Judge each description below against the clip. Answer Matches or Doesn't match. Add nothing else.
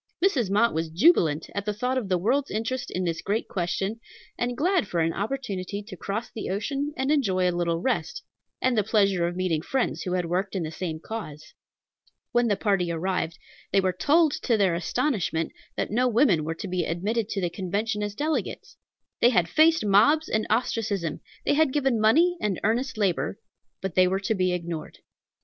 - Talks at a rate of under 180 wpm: Doesn't match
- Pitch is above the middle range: Matches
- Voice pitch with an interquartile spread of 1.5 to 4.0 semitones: Doesn't match